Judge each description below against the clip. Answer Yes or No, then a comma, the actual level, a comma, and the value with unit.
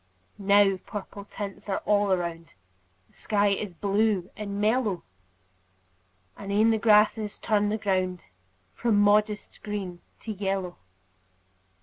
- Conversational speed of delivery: No, slow, 120 wpm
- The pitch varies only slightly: Yes, narrow, 1.6 semitones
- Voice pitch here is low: No, high, 205 Hz